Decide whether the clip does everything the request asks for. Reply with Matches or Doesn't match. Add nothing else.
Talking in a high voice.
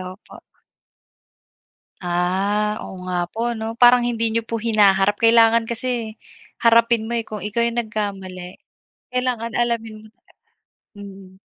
Matches